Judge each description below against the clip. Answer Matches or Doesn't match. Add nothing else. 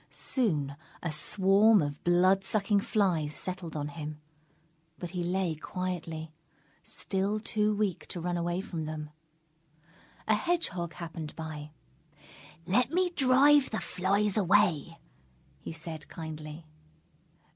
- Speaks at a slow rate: Matches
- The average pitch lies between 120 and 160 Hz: Doesn't match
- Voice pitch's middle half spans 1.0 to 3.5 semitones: Doesn't match